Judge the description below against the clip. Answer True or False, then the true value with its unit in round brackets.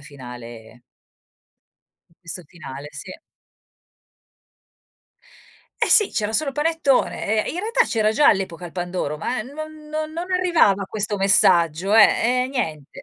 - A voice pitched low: False (205 Hz)